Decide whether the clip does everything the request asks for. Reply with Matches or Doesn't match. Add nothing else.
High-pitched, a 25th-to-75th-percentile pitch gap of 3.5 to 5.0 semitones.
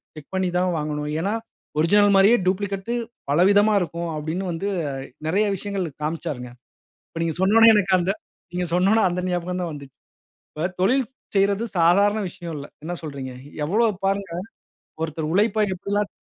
Doesn't match